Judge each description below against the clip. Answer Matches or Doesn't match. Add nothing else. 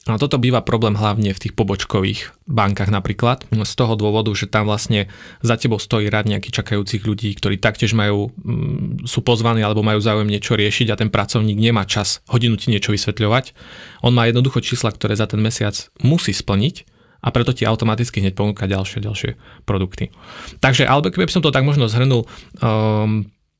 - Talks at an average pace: Doesn't match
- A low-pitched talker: Matches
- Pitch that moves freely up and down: Doesn't match